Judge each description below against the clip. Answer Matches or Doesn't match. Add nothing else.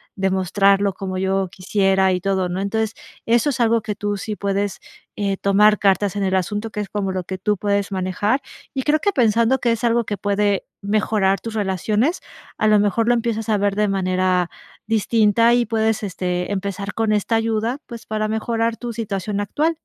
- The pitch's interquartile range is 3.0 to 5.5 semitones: Doesn't match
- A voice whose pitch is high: Matches